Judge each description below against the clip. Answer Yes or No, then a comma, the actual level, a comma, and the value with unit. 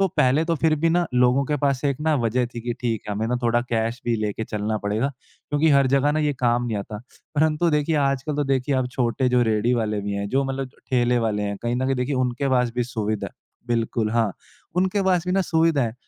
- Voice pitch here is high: No, low, 125 Hz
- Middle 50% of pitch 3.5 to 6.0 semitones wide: Yes, average, 3.9 semitones